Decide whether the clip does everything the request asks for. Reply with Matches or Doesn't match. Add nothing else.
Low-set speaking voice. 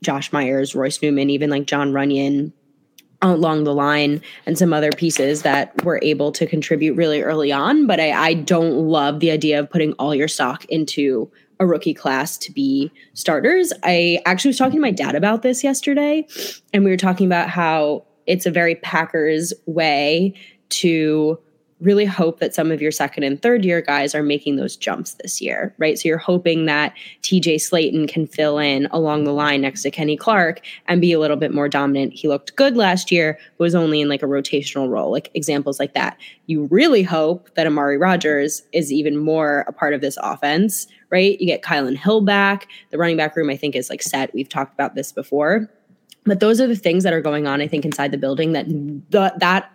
Doesn't match